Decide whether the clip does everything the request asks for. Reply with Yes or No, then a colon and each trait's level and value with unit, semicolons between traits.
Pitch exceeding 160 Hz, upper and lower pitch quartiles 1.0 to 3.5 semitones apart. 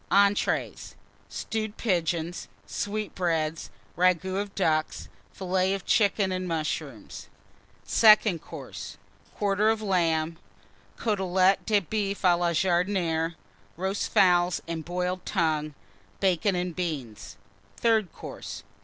Yes: medium, 185 Hz; average, 3.0 semitones